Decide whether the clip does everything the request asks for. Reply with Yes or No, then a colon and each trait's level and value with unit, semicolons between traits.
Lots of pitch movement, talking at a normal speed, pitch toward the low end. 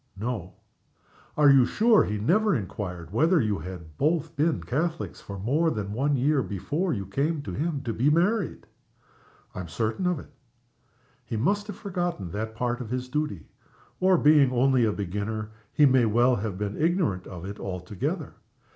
Yes: wide, 7.5 semitones; average, 175 wpm; low, 125 Hz